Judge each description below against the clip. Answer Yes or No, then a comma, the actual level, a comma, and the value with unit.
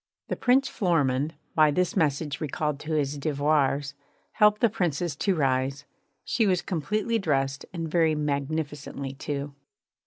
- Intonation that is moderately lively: Yes, average, 3.8 semitones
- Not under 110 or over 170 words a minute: Yes, slow, 135 wpm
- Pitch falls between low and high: Yes, medium, 150 Hz